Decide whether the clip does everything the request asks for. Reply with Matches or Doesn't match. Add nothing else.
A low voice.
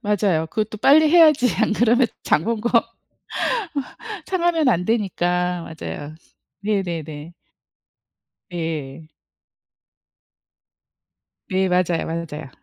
Doesn't match